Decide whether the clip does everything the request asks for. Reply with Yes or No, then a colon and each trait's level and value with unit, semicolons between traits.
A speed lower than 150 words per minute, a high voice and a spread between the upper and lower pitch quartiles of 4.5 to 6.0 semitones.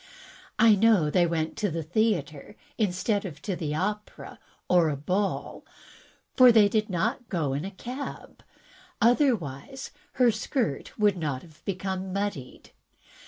Yes: average, 140 wpm; high, 195 Hz; average, 5.2 semitones